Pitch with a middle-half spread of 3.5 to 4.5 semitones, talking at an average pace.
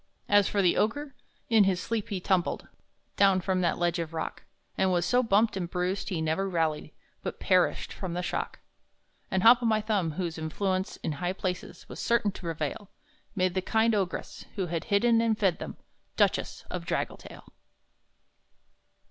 No: average, 3.1 semitones; average, 175 wpm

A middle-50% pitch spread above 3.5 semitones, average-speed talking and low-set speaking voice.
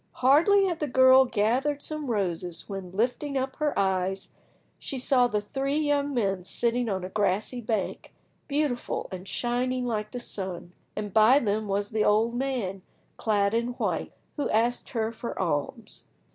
No: average, 4.6 semitones; average, 160 wpm; high, 230 Hz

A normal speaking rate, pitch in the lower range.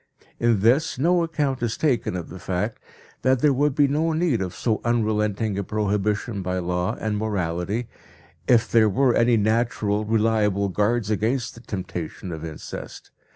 Yes: average, 160 wpm; low, 110 Hz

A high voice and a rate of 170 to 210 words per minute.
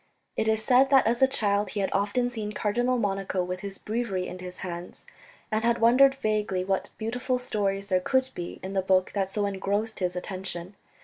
Yes: high, 205 Hz; average, 200 wpm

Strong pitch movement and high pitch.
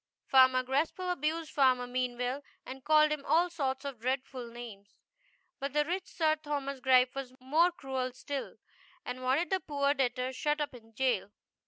No: average, 3.0 semitones; very high, 270 Hz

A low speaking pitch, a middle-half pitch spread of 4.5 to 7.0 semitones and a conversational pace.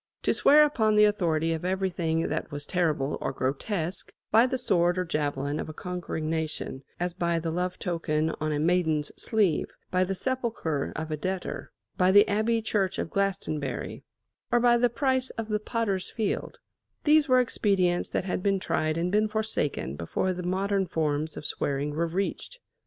No: medium, 180 Hz; average, 5.0 semitones; average, 180 wpm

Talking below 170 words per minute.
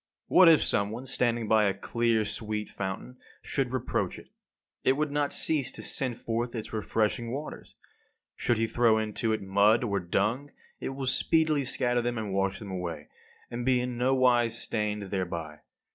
No: average, 175 wpm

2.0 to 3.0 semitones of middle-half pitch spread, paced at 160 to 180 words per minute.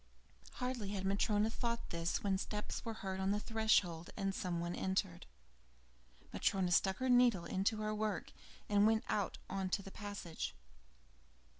No: narrow, 2.5 semitones; average, 150 wpm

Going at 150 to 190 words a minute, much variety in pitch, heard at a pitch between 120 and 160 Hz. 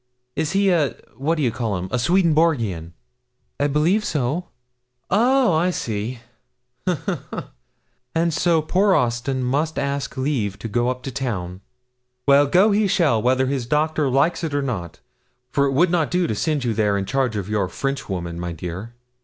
Yes: average, 175 wpm; wide, 6.2 semitones; low, 135 Hz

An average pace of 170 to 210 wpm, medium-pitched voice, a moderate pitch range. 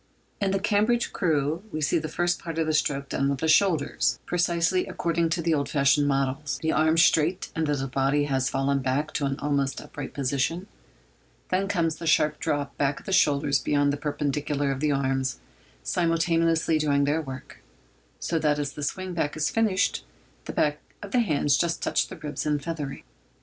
Yes: average, 185 wpm; medium, 150 Hz; average, 3.0 semitones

